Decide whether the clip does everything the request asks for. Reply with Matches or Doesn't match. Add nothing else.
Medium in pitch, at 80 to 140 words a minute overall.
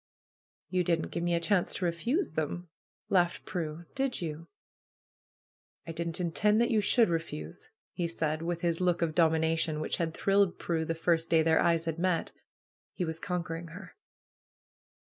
Doesn't match